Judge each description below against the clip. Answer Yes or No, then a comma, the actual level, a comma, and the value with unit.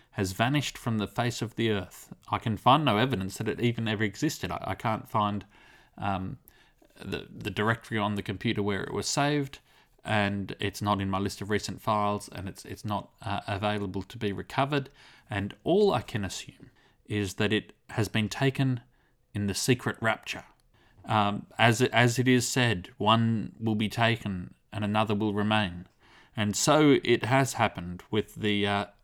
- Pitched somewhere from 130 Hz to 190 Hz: No, low, 110 Hz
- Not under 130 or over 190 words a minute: Yes, average, 185 wpm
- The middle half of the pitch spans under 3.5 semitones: Yes, average, 3.0 semitones